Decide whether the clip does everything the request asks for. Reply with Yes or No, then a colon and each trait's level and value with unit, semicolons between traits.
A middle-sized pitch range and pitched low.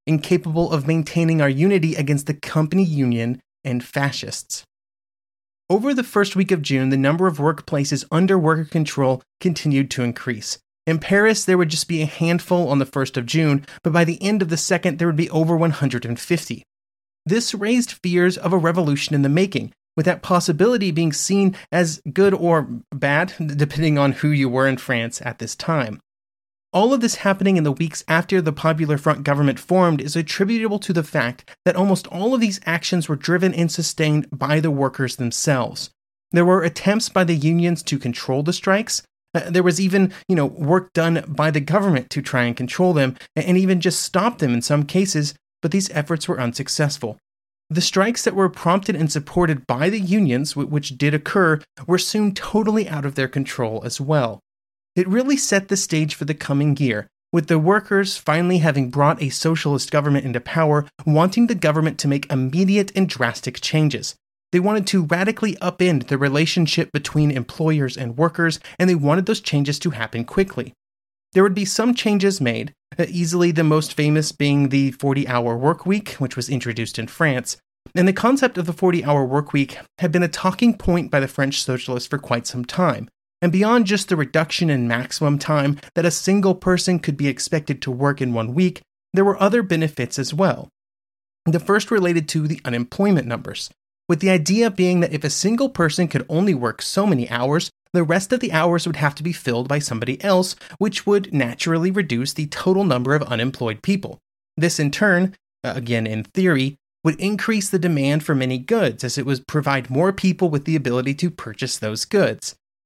No: average, 4.9 semitones; medium, 160 Hz